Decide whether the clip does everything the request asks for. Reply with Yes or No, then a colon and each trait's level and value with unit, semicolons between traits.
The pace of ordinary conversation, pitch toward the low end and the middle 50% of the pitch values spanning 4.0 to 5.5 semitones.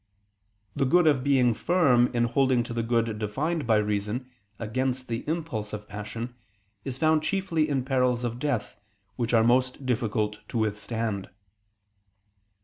No: average, 145 wpm; low, 120 Hz; average, 3.4 semitones